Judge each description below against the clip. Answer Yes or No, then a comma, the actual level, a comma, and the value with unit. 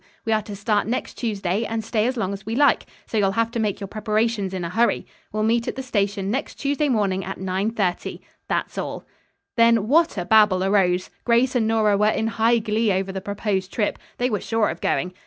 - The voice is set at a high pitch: Yes, high, 215 Hz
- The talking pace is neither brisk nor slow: No, fast, 220 wpm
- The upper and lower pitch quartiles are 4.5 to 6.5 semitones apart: No, average, 2.8 semitones